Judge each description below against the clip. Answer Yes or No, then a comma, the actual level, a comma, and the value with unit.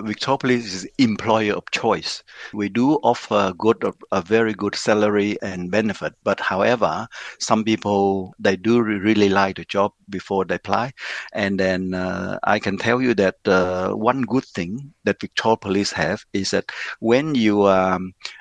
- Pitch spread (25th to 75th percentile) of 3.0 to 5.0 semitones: No, narrow, 2.4 semitones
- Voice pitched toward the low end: Yes, low, 100 Hz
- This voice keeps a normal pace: No, fast, 165 wpm